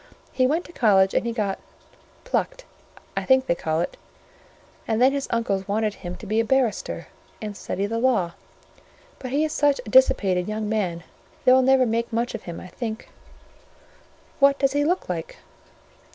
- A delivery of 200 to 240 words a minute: No, average, 180 wpm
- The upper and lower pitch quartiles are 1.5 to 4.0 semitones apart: No, average, 4.8 semitones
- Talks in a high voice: Yes, high, 230 Hz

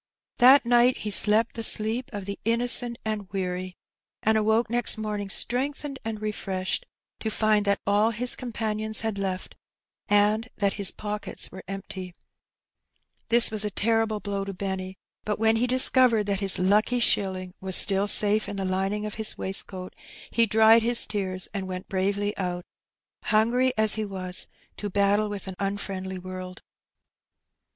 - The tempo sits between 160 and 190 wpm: Yes, average, 165 wpm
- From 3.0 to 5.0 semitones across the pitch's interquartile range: No, narrow, 2.5 semitones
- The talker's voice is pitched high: Yes, high, 210 Hz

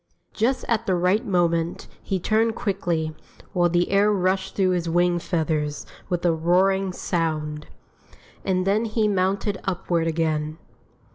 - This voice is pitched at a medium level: Yes, medium, 180 Hz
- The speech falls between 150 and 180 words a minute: No, average, 140 wpm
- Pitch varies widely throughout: No, average, 2.9 semitones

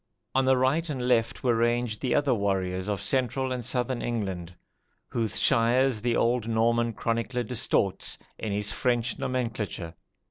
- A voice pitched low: Yes, low, 120 Hz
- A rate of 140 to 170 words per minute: Yes, average, 150 wpm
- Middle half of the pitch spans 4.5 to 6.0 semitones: No, average, 2.9 semitones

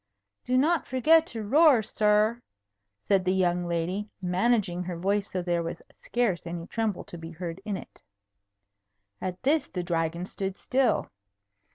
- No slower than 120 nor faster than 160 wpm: Yes, average, 155 wpm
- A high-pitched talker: Yes, high, 195 Hz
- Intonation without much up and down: No, average, 5.1 semitones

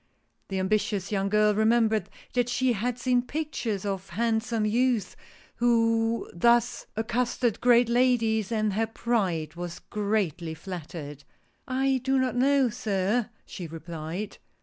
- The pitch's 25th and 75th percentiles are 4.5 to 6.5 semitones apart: No, average, 3.9 semitones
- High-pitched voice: Yes, high, 220 Hz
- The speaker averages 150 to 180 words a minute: No, slow, 135 wpm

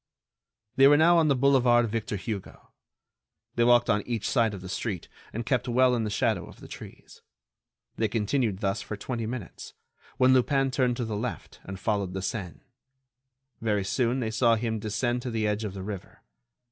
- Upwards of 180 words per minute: Yes, average, 195 wpm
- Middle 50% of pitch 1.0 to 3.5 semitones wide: Yes, average, 3.1 semitones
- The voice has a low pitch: Yes, low, 115 Hz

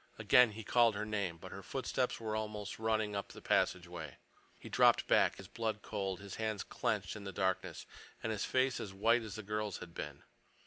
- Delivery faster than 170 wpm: Yes, average, 200 wpm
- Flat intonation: Yes, narrow, 2.2 semitones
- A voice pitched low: Yes, low, 105 Hz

